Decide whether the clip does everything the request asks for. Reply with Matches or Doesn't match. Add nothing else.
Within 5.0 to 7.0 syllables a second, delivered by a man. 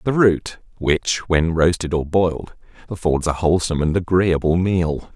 Doesn't match